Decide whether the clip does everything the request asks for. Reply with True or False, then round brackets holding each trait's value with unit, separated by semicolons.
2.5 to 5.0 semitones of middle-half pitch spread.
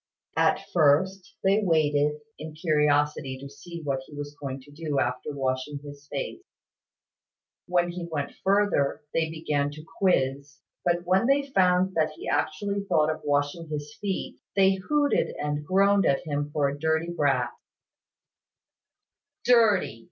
True (4.2 semitones)